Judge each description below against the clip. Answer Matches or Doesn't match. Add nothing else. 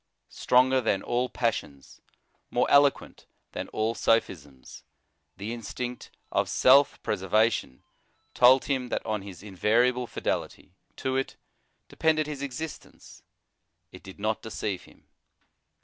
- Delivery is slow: Matches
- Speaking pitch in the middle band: Doesn't match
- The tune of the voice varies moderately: Matches